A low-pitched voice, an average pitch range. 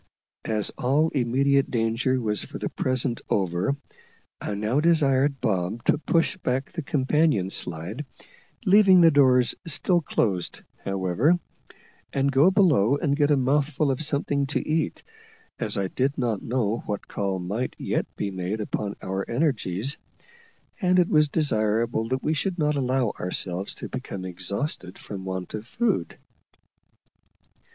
No: low, 130 Hz; wide, 6.3 semitones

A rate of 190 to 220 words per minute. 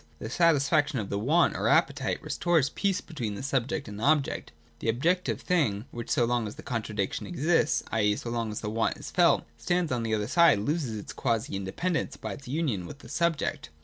Yes: fast, 205 wpm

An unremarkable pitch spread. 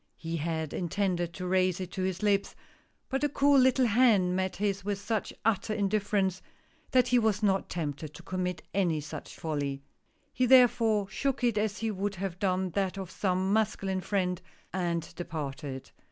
Yes: average, 3.2 semitones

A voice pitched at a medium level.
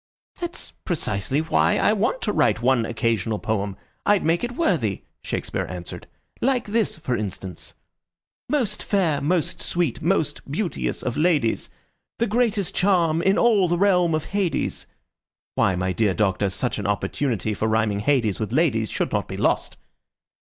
Yes: medium, 150 Hz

